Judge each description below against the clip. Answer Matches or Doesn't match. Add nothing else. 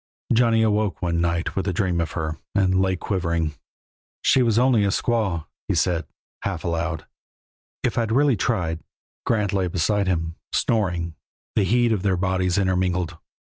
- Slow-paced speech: Doesn't match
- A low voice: Matches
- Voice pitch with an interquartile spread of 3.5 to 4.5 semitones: Matches